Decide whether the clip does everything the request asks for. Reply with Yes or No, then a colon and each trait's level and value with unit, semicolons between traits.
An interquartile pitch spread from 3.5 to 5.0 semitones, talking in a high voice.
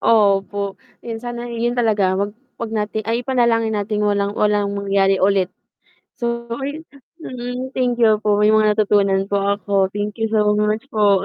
No: average, 2.7 semitones; high, 210 Hz